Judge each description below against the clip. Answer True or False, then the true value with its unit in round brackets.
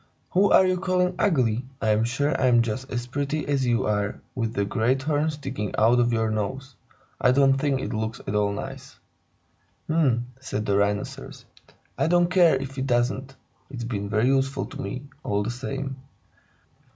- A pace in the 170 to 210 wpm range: True (180 wpm)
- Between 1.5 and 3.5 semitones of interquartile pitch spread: False (3.9 semitones)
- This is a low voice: True (130 Hz)